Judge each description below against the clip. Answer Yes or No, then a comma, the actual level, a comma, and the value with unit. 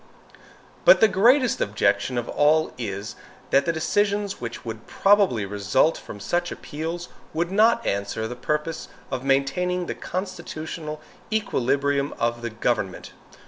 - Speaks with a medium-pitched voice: Yes, medium, 150 Hz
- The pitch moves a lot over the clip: Yes, wide, 7.4 semitones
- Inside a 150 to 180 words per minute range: No, slow, 135 wpm